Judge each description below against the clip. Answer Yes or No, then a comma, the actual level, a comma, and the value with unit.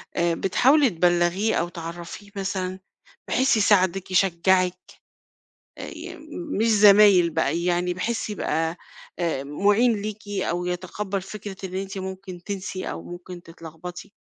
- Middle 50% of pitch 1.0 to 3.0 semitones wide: Yes, average, 2.7 semitones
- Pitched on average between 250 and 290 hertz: No, medium, 185 Hz